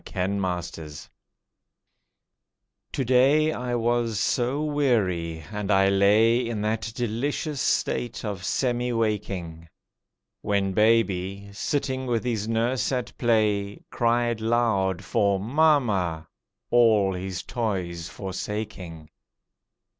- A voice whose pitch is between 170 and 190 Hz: No, low, 110 Hz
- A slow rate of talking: Yes, slow, 100 wpm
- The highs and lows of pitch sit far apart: No, average, 3.9 semitones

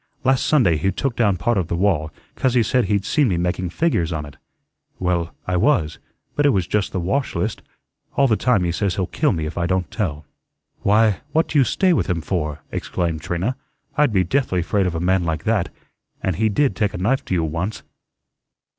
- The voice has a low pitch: Yes, very low, 95 Hz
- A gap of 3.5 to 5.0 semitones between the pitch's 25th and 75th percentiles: No, wide, 5.6 semitones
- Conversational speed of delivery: No, fast, 220 wpm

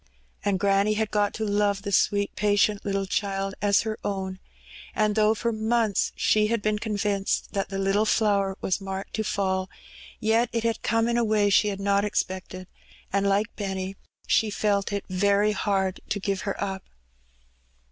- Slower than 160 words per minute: No, average, 175 wpm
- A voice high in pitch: Yes, high, 205 Hz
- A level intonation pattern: Yes, narrow, 1.5 semitones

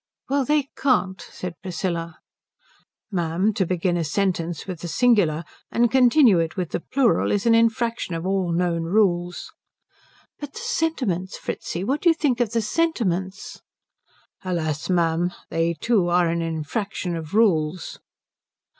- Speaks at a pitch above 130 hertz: Yes, medium, 185 Hz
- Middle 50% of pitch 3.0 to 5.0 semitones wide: No, wide, 5.5 semitones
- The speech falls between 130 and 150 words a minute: Yes, average, 145 wpm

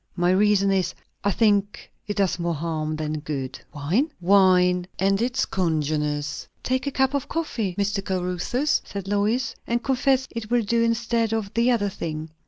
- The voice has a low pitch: No, high, 200 Hz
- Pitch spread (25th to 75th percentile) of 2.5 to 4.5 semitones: No, average, 5.1 semitones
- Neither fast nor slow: Yes, average, 170 wpm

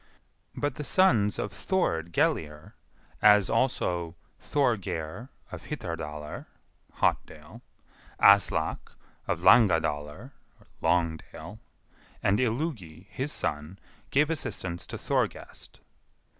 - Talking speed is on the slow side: Yes, slow, 90 wpm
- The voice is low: Yes, low, 100 Hz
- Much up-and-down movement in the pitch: Yes, wide, 7.9 semitones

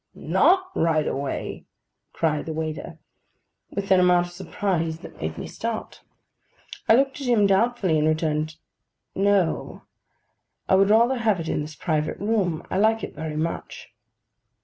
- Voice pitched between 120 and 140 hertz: No, medium, 180 Hz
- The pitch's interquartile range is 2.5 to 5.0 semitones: No, wide, 5.4 semitones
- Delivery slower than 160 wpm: Yes, average, 150 wpm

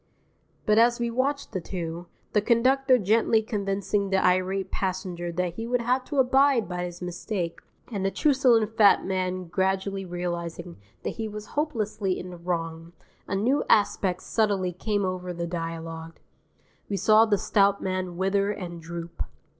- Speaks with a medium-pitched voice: No, high, 195 Hz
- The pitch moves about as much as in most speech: Yes, average, 3.8 semitones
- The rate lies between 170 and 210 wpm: No, average, 160 wpm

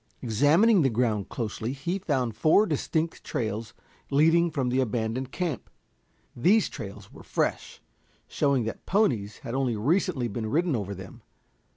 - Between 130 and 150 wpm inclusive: Yes, average, 145 wpm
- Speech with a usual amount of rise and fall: No, wide, 6.4 semitones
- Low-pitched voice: Yes, low, 130 Hz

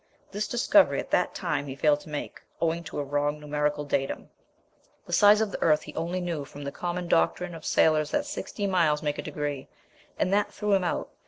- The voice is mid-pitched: Yes, medium, 155 Hz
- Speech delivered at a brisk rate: Yes, fast, 215 wpm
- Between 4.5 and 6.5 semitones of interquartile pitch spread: No, average, 3.9 semitones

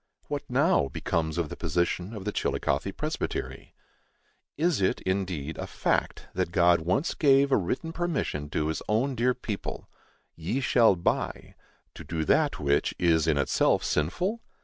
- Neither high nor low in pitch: No, very low, 90 Hz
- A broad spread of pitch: Yes, wide, 8.0 semitones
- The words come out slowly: No, average, 155 wpm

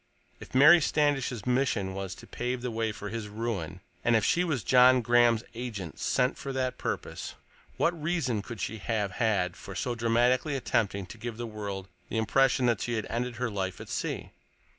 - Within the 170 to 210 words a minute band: Yes, average, 190 wpm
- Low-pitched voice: Yes, low, 115 Hz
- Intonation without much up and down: No, average, 3.3 semitones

